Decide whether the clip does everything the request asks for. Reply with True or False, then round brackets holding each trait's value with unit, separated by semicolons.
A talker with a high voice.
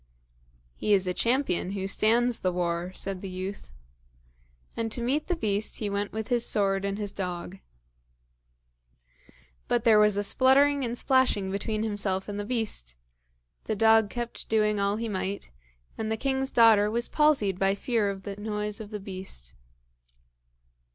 True (210 Hz)